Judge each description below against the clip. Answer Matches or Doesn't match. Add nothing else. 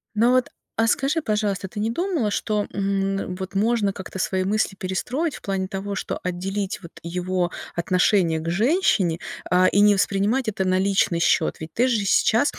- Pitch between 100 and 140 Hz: Doesn't match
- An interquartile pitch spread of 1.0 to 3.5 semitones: Matches